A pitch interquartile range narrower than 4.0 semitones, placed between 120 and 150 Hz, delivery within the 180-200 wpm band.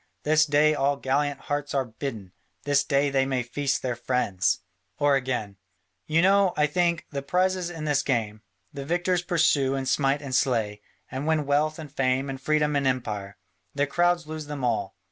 Yes: average, 2.9 semitones; medium, 140 Hz; average, 185 wpm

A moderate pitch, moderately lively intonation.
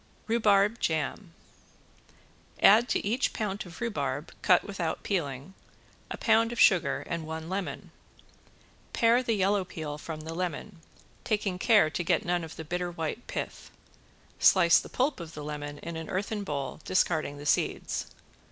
Yes: medium, 180 Hz; average, 4.7 semitones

